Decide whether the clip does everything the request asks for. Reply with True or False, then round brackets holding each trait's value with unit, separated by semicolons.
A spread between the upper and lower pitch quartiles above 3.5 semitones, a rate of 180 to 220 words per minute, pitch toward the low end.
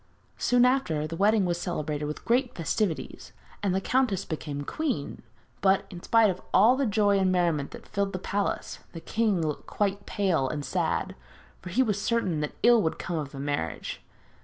False (5.4 semitones; 185 wpm; 190 Hz)